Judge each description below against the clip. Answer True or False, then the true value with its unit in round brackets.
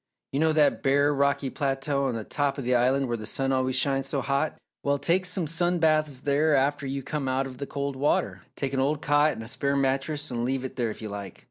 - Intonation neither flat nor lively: False (1.8 semitones)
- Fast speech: True (245 wpm)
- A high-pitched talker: False (140 Hz)